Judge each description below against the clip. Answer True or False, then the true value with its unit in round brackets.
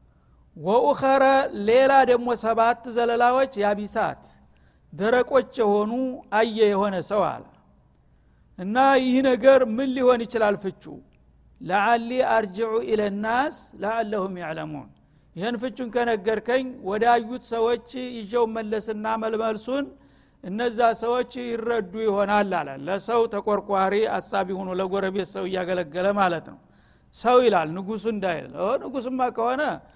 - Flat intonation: False (3.9 semitones)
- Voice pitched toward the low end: False (225 Hz)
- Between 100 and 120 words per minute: True (105 wpm)